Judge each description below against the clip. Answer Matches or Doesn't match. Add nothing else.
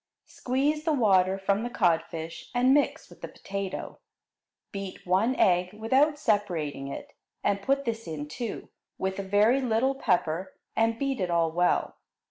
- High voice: Matches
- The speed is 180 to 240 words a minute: Doesn't match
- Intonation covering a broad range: Matches